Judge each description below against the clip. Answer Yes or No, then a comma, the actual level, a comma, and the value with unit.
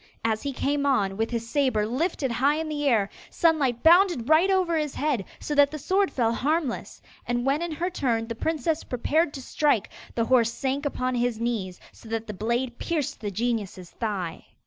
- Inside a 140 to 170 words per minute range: No, average, 195 wpm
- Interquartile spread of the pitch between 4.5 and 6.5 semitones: Yes, average, 5.0 semitones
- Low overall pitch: No, very high, 260 Hz